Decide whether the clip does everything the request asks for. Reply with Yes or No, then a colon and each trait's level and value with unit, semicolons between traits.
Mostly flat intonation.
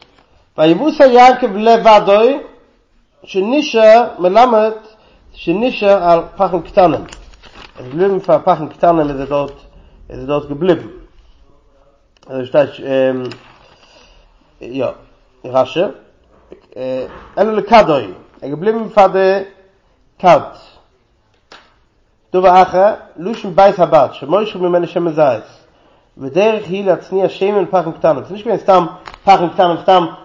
No: average, 4.3 semitones